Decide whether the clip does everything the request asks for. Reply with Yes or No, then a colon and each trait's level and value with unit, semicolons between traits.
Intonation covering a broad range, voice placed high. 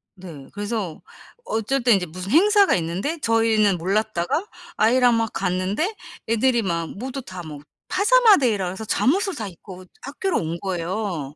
Yes: wide, 6.2 semitones; high, 215 Hz